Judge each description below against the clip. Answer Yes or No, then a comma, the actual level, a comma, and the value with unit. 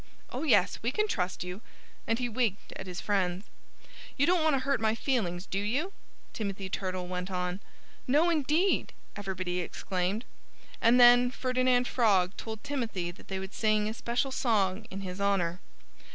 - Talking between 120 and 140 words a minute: No, average, 165 wpm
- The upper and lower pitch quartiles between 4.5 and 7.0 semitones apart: Yes, average, 5.2 semitones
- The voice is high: Yes, high, 215 Hz